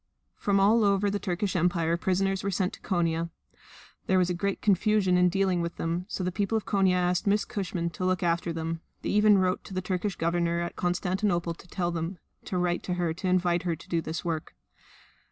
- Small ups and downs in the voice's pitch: Yes, narrow, 2.2 semitones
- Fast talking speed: Yes, fast, 210 wpm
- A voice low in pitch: No, medium, 180 Hz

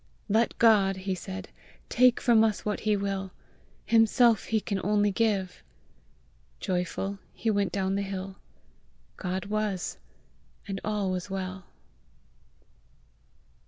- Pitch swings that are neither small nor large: No, narrow, 2.0 semitones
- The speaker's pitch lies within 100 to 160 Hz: No, high, 200 Hz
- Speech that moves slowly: Yes, slow, 120 wpm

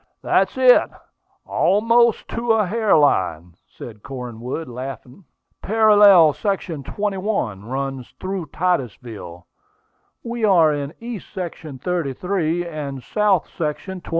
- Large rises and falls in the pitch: Yes, wide, 7.5 semitones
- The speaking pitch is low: No, medium, 165 Hz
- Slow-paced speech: Yes, slow, 115 wpm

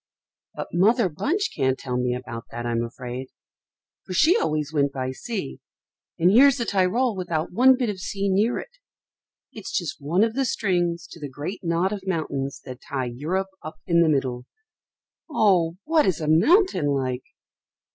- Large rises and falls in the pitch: Yes, wide, 7.4 semitones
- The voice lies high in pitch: No, medium, 170 Hz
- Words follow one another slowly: No, average, 175 wpm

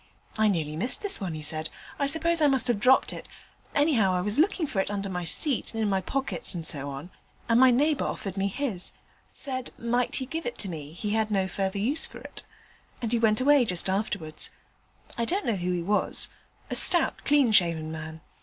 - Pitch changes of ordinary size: No, wide, 6.5 semitones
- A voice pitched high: Yes, high, 215 Hz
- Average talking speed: No, fast, 215 wpm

